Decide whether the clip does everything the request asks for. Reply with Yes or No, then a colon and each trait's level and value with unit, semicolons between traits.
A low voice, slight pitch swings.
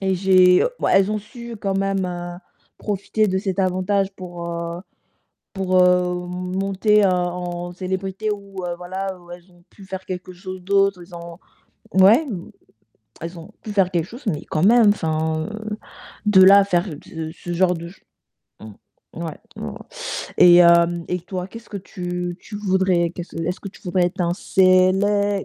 No: medium, 185 Hz; narrow, 1.9 semitones